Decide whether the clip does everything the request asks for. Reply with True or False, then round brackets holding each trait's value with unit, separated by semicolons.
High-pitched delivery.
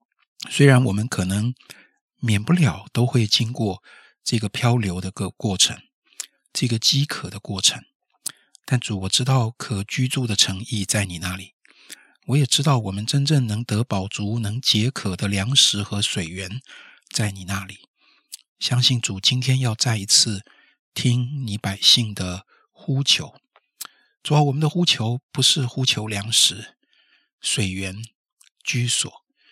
False (115 Hz)